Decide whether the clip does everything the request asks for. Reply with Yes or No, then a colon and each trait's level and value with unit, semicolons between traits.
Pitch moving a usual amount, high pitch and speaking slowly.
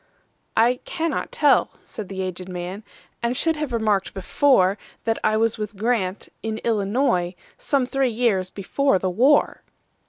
Yes: average, 4.7 semitones; high, 220 Hz; slow, 125 wpm